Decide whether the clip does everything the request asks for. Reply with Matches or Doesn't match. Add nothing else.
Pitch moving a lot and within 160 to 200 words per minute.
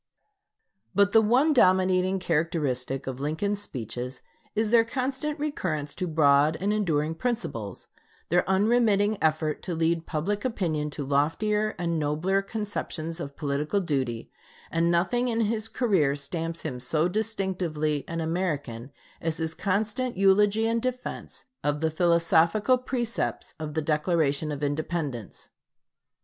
Doesn't match